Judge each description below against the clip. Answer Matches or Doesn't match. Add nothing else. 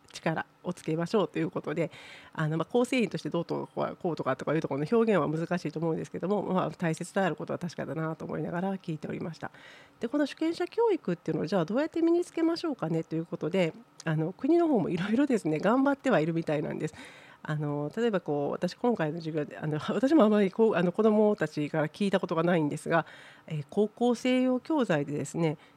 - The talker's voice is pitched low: Doesn't match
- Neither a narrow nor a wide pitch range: Doesn't match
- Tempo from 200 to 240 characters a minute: Doesn't match